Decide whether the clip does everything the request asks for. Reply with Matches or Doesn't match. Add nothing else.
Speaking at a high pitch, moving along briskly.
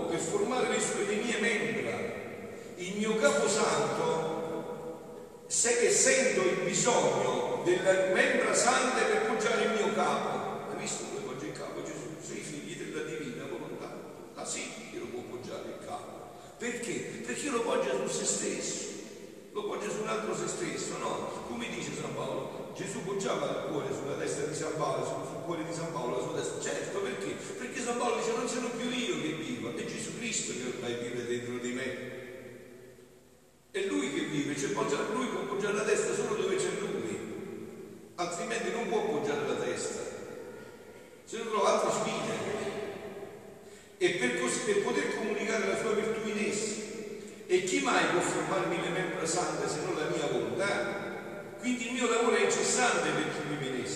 Matches